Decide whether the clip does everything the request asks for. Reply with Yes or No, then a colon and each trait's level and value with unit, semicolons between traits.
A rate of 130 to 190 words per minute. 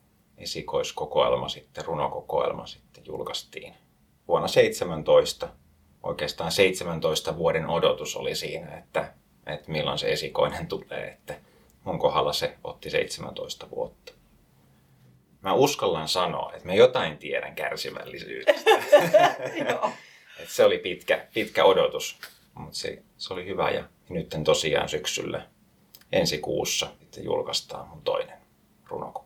No: average, 110 wpm